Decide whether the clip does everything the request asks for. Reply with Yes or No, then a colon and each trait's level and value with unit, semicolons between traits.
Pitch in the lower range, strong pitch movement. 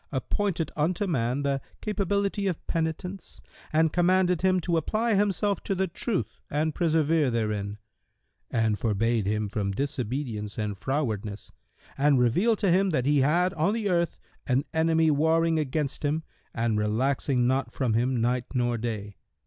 No: medium, 145 Hz; wide, 6.8 semitones